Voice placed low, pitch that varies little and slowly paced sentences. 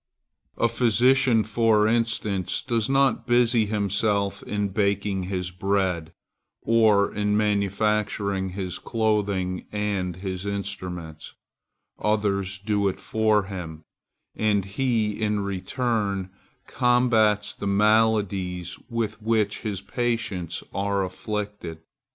Yes: low, 105 Hz; narrow, 2.3 semitones; slow, 105 wpm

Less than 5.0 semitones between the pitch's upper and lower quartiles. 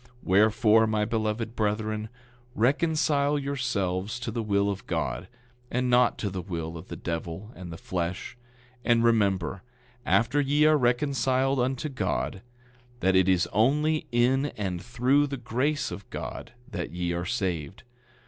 No: wide, 5.5 semitones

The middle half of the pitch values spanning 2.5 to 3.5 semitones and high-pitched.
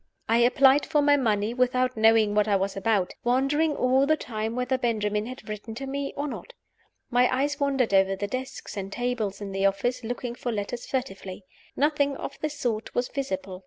No: average, 4.4 semitones; high, 245 Hz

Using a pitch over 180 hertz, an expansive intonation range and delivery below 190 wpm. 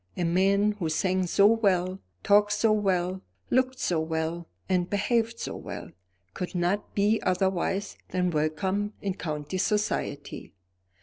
No: high, 190 Hz; average, 2.9 semitones; slow, 135 wpm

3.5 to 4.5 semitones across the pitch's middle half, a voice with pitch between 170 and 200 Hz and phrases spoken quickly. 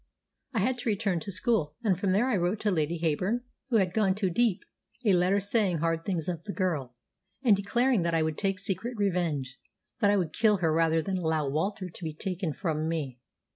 Yes: average, 3.9 semitones; medium, 185 Hz; fast, 215 wpm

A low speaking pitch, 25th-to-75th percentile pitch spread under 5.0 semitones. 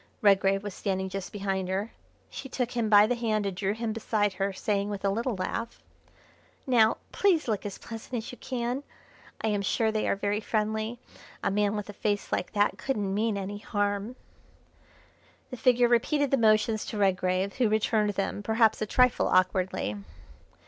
No: high, 210 Hz; narrow, 2.5 semitones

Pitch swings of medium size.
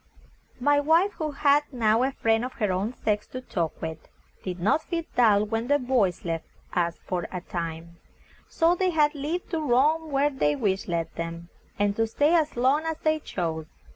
No: wide, 8.6 semitones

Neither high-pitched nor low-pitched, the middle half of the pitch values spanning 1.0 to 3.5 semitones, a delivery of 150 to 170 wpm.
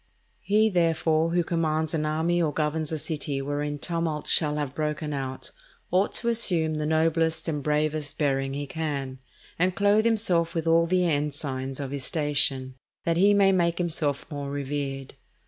Yes: medium, 155 Hz; narrow, 2.6 semitones; average, 165 wpm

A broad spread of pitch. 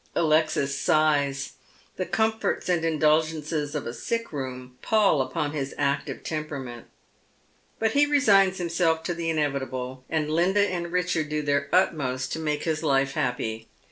No: average, 3.7 semitones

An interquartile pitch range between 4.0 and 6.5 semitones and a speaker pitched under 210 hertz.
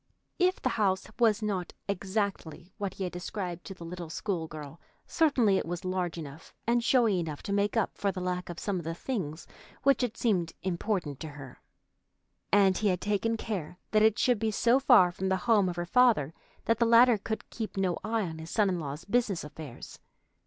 Yes: average, 4.3 semitones; high, 190 Hz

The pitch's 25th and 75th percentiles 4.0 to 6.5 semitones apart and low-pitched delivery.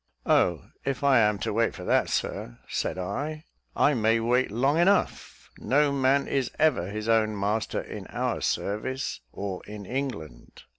Yes: average, 4.9 semitones; low, 115 Hz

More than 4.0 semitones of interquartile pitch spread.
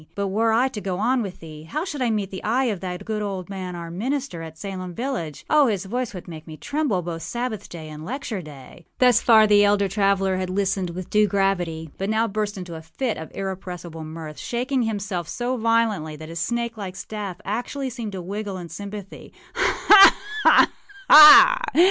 Yes: average, 4.6 semitones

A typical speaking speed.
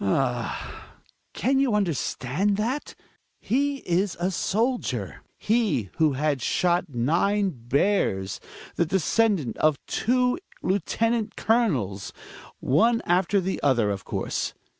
No: slow, 110 wpm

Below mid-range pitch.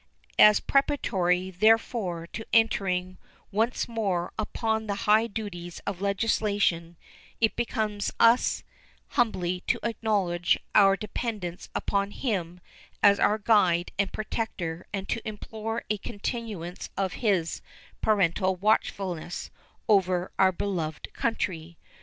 No: high, 200 Hz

